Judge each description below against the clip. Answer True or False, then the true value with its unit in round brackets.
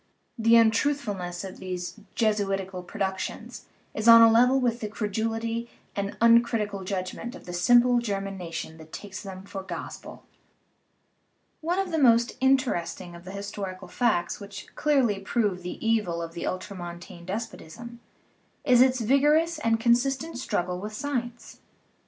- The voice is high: True (215 Hz)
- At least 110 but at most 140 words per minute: False (150 wpm)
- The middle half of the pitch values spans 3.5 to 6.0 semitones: True (4.2 semitones)